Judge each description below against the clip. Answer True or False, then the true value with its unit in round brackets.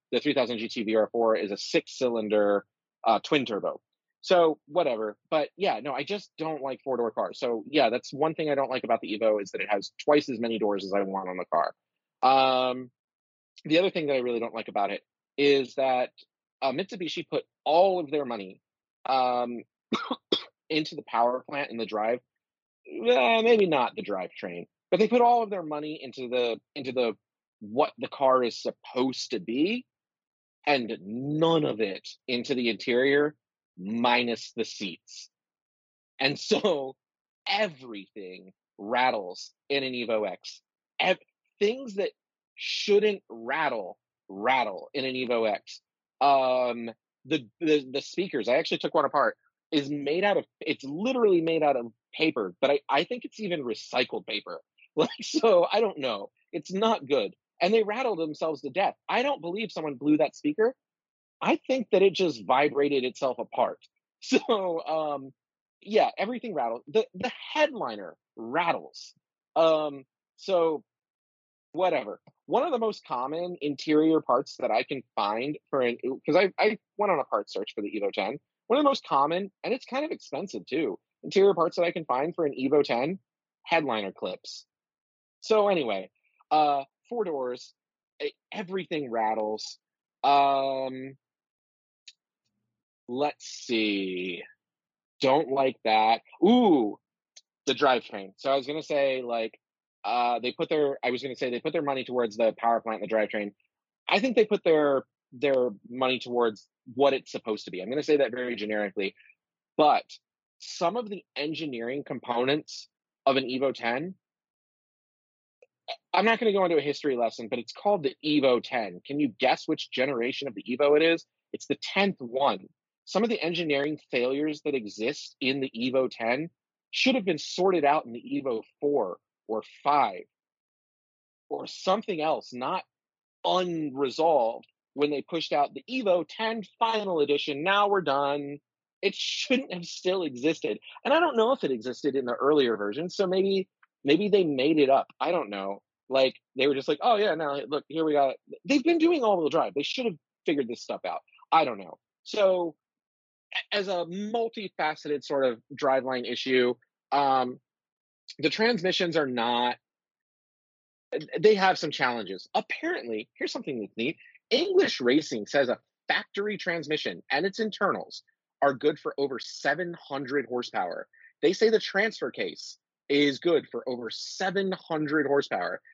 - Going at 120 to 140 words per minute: False (165 wpm)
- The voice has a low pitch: False (145 Hz)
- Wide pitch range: True (7.3 semitones)